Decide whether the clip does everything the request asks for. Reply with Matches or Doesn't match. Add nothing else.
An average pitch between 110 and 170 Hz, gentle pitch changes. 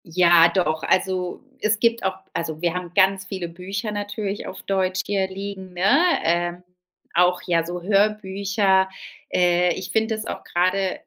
Doesn't match